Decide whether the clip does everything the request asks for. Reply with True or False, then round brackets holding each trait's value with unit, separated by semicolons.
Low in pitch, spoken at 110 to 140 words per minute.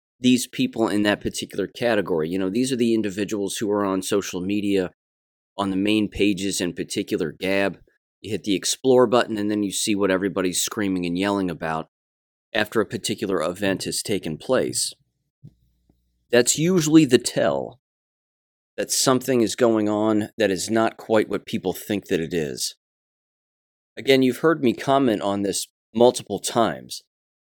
False (100 Hz; 160 wpm)